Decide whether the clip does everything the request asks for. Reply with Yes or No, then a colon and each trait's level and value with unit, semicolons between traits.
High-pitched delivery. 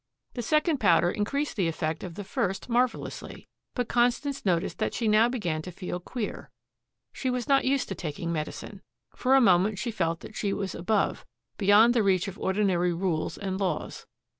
Yes: high, 200 Hz